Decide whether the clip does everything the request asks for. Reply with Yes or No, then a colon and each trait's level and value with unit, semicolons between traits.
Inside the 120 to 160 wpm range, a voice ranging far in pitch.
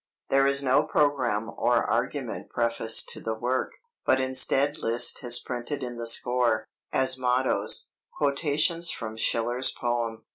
No: average, 140 wpm; average, 2.7 semitones